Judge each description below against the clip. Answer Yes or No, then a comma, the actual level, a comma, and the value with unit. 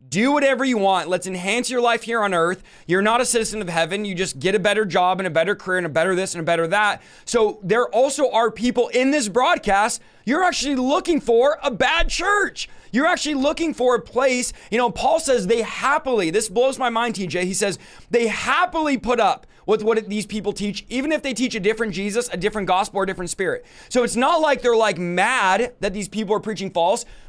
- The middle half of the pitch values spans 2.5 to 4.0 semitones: No, average, 4.8 semitones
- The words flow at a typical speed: No, fast, 230 wpm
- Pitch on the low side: No, high, 230 Hz